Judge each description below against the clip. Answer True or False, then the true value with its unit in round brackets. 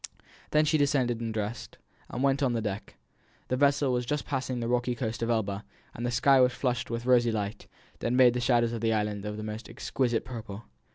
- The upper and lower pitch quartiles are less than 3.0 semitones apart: True (2.4 semitones)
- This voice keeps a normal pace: False (215 wpm)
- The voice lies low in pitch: True (120 Hz)